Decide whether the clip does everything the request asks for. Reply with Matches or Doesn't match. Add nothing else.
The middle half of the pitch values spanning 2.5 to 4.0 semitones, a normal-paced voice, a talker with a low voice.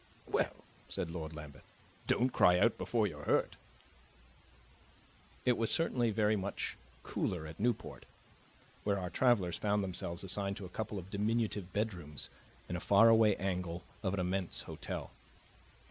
Matches